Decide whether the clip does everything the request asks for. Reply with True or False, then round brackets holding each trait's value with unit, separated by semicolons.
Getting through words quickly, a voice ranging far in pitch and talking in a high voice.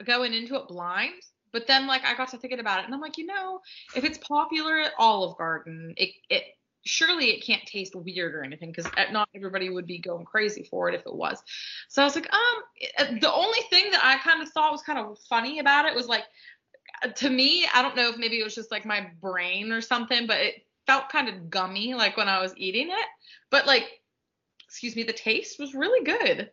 True (230 wpm; 7.3 semitones; 245 Hz)